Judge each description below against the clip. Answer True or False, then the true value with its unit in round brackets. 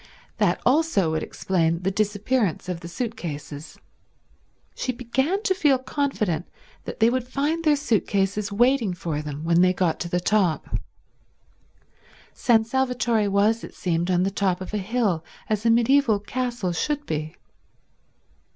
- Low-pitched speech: False (210 Hz)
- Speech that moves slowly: False (160 wpm)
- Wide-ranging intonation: True (5.9 semitones)